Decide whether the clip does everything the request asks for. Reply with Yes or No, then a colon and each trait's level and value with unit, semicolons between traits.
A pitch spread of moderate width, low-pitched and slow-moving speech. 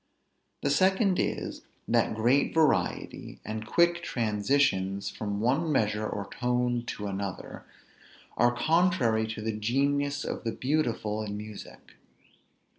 Yes: average, 5.0 semitones; low, 120 Hz; slow, 120 wpm